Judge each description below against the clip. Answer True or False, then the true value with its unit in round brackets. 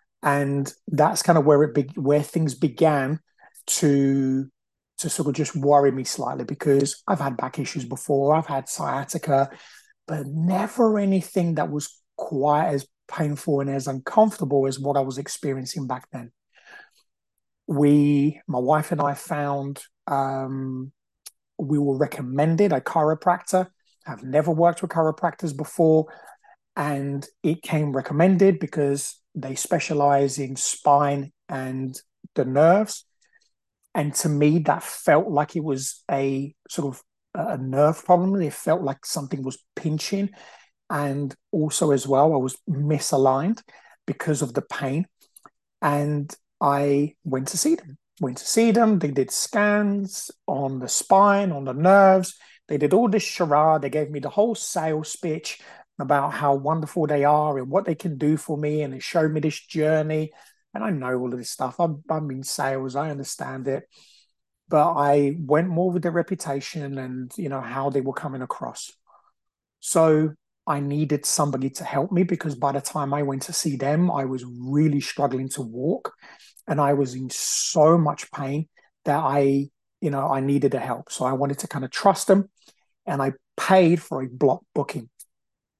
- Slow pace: False (165 wpm)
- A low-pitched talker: False (145 Hz)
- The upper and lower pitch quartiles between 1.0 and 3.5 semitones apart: True (3.2 semitones)